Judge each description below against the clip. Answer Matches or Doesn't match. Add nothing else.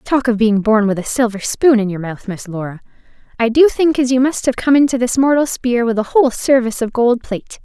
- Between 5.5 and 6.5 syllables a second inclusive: Matches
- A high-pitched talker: Matches